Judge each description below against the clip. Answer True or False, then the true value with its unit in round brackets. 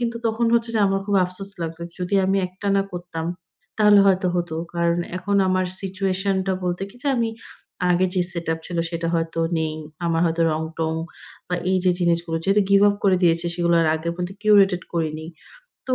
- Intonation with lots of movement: False (2.7 semitones)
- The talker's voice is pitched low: False (180 Hz)